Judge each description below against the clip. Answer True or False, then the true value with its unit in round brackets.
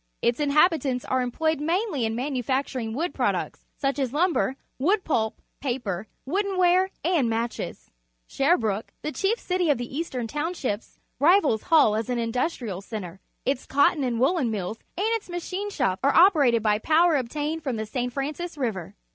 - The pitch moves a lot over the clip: True (6.3 semitones)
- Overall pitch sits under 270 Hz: False (275 Hz)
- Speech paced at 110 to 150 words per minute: False (160 wpm)